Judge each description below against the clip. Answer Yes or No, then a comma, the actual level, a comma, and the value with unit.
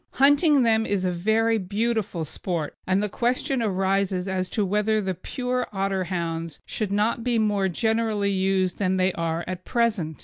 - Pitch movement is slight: No, average, 3.3 semitones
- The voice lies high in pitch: Yes, high, 200 Hz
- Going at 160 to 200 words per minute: Yes, average, 165 wpm